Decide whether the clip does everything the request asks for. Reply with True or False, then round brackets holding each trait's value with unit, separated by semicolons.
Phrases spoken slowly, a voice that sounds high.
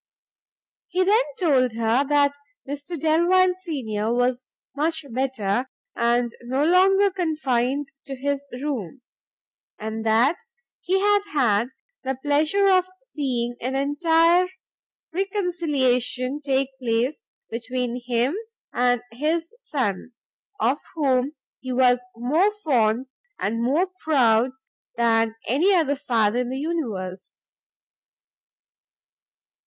True (105 wpm; 270 Hz)